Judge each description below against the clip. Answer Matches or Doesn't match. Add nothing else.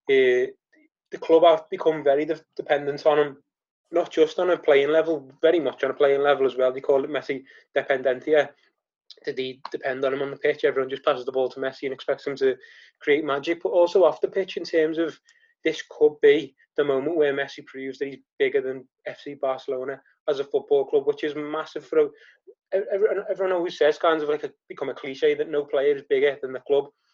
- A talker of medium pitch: Matches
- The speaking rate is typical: Doesn't match